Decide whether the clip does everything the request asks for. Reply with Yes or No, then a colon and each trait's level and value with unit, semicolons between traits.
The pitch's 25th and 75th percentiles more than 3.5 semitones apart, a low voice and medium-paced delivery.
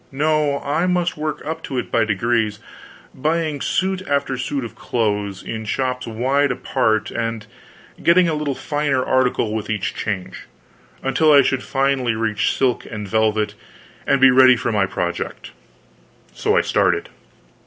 Yes: average, 4.6 semitones; low, 130 Hz; average, 155 wpm